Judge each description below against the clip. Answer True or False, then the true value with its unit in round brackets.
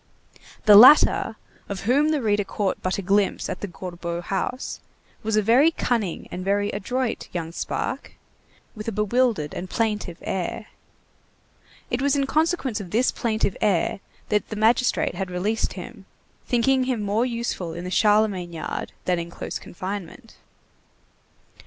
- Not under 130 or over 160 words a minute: True (150 wpm)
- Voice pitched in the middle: False (210 Hz)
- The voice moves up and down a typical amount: True (4.4 semitones)